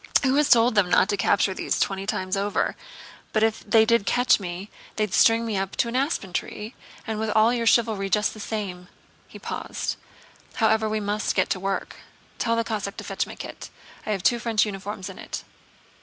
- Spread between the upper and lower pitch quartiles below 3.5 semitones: Yes, narrow, 2.6 semitones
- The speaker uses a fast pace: Yes, fast, 210 wpm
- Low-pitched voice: No, high, 215 Hz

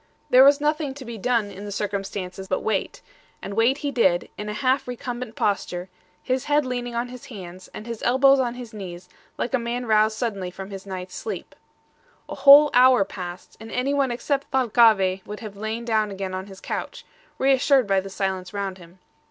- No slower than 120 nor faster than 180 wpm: No, average, 195 wpm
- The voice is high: Yes, high, 220 Hz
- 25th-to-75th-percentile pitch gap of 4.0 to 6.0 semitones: Yes, average, 4.6 semitones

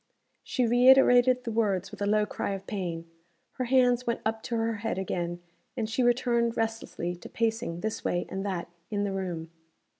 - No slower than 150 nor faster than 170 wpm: No, average, 185 wpm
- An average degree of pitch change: Yes, average, 3.8 semitones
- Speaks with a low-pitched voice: No, high, 220 Hz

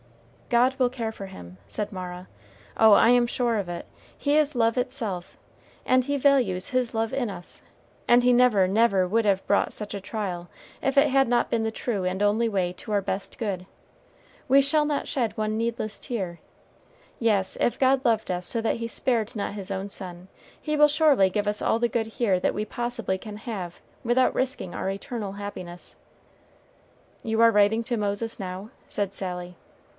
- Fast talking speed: No, average, 190 wpm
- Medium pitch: No, high, 220 Hz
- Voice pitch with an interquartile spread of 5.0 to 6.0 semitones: No, average, 4.0 semitones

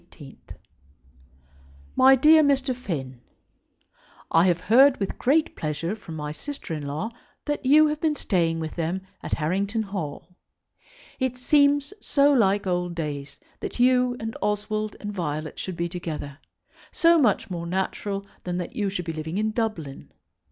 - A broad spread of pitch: Yes, wide, 7.3 semitones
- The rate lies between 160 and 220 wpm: No, average, 150 wpm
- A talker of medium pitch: No, high, 200 Hz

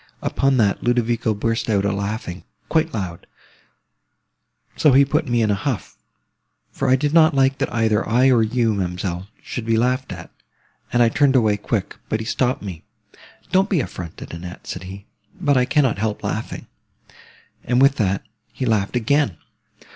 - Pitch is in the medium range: No, low, 115 Hz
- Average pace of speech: Yes, average, 170 wpm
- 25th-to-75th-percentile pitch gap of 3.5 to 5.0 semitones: Yes, average, 4.6 semitones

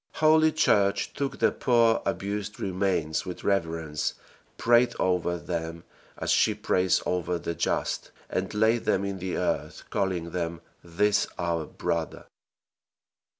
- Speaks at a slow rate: Yes, slow, 130 wpm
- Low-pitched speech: Yes, very low, 95 Hz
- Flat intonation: No, average, 3.7 semitones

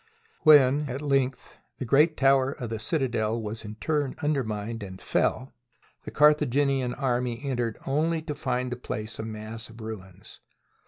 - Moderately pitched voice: No, low, 125 Hz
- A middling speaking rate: Yes, average, 160 wpm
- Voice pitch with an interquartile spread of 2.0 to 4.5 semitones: Yes, average, 3.9 semitones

